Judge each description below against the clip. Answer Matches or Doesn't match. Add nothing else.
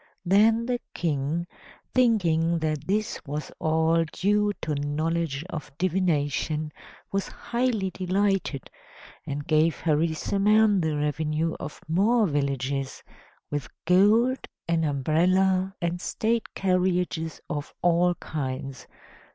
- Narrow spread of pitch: Doesn't match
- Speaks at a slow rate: Matches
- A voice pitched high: Doesn't match